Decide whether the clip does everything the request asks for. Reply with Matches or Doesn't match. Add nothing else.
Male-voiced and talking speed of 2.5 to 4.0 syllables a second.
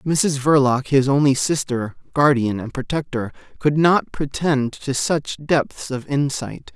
Matches